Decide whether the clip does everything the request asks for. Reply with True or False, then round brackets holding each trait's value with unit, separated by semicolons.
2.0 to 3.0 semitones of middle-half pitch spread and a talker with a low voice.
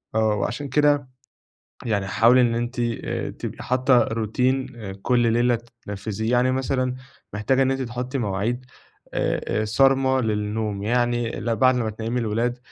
True (2.6 semitones; 120 Hz)